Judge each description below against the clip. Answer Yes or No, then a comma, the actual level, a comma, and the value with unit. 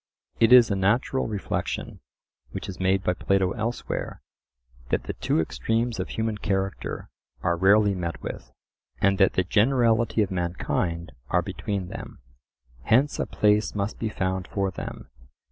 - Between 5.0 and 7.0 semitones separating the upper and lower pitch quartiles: No, average, 3.1 semitones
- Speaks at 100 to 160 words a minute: Yes, average, 150 wpm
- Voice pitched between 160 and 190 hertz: No, low, 100 Hz